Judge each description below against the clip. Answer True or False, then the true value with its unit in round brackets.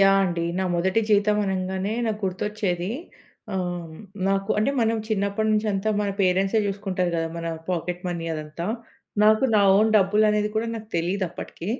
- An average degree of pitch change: True (3.0 semitones)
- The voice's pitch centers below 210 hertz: True (195 Hz)